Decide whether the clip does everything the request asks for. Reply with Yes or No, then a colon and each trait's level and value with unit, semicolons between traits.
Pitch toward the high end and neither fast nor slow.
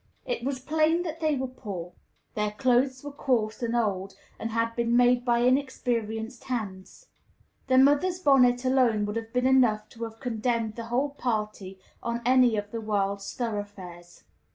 Yes: high, 235 Hz; average, 165 wpm